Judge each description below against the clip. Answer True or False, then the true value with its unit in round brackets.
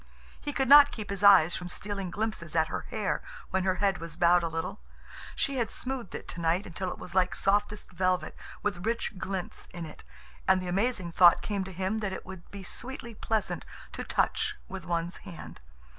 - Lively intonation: False (2.9 semitones)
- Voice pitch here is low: False (190 Hz)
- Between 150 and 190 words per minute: False (200 wpm)